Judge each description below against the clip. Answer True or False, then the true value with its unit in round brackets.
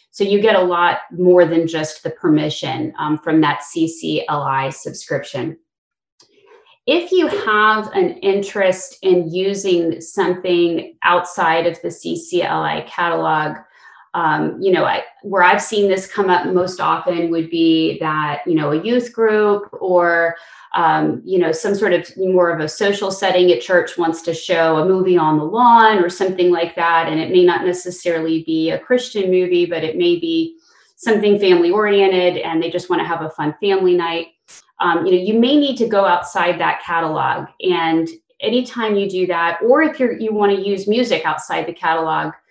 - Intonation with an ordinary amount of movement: True (4.0 semitones)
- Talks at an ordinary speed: True (180 wpm)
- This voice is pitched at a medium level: True (180 Hz)